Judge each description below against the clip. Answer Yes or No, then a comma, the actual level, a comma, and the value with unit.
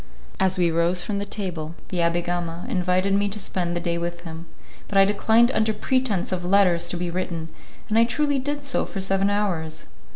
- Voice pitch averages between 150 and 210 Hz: Yes, medium, 185 Hz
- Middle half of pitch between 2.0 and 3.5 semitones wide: Yes, average, 3.1 semitones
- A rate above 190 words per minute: Yes, fast, 205 wpm